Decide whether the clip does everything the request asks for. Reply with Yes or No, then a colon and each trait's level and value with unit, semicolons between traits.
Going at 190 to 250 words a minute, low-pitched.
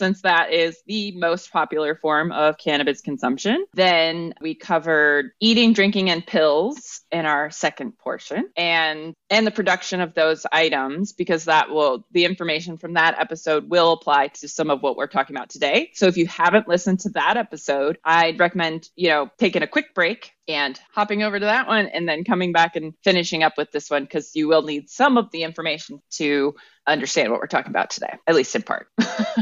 No: average, 200 wpm; medium, 165 Hz